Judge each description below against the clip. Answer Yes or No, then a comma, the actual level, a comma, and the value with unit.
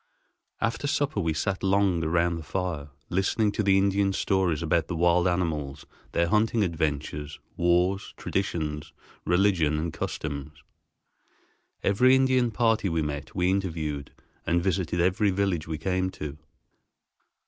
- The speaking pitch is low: Yes, very low, 90 Hz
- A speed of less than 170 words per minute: Yes, slow, 135 wpm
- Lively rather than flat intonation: No, average, 3.9 semitones